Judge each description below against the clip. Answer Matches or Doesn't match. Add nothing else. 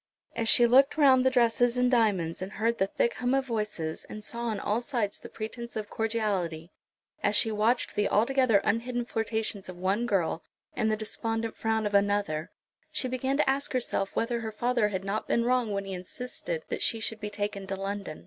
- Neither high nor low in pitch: Doesn't match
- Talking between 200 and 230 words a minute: Matches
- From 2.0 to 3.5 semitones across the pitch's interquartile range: Matches